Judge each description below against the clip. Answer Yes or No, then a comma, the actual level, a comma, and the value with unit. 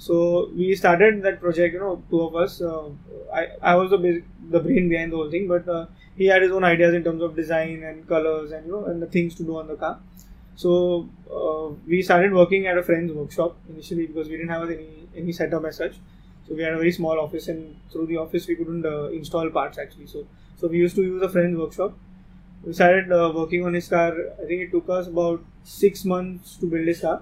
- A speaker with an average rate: No, fast, 240 wpm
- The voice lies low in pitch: No, medium, 170 Hz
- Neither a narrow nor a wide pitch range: No, narrow, 1.6 semitones